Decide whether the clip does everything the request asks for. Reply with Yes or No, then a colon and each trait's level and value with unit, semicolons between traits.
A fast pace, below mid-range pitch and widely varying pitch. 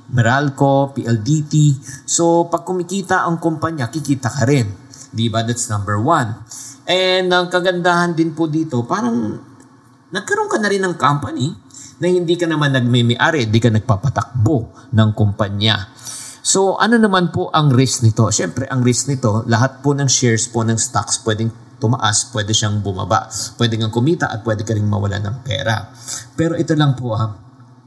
No: average, 160 wpm; low, 130 Hz; wide, 5.7 semitones